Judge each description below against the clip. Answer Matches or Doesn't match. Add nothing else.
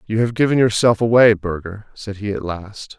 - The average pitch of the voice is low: Matches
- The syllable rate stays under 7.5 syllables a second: Matches